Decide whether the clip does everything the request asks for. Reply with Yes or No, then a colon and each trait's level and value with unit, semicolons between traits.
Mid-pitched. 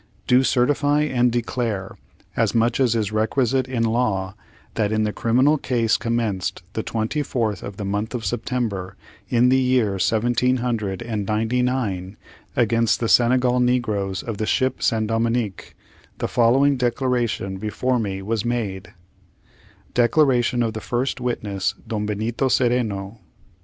No: low, 115 Hz